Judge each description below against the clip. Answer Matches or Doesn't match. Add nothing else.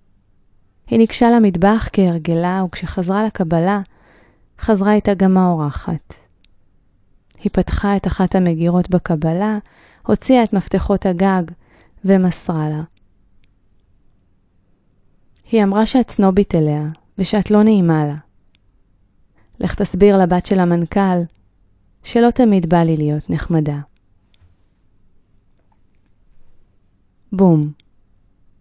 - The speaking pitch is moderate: Matches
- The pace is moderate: Doesn't match